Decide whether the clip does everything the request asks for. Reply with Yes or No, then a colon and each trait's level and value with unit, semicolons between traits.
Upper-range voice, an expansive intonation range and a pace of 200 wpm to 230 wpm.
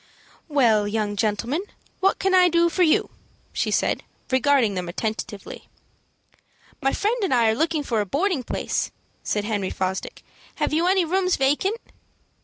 No: very high, 275 Hz; wide, 8.8 semitones; average, 155 wpm